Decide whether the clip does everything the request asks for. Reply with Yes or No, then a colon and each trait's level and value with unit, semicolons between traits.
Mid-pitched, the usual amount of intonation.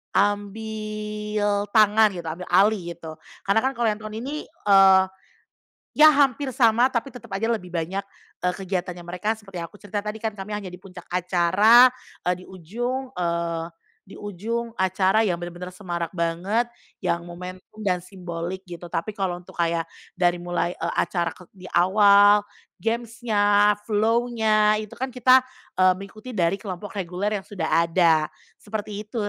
No: high, 200 Hz; average, 3.5 semitones